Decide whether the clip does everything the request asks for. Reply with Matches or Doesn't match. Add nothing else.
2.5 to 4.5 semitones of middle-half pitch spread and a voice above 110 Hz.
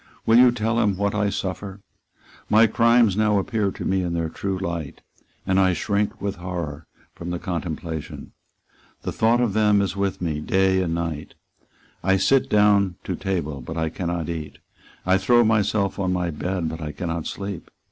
Doesn't match